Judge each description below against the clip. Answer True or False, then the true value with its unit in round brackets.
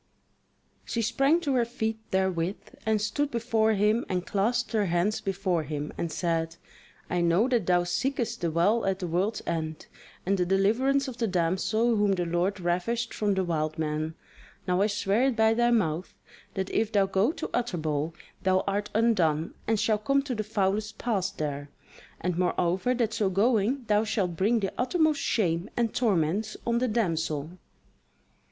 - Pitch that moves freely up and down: False (4.7 semitones)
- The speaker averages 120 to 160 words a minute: False (175 wpm)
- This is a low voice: False (200 Hz)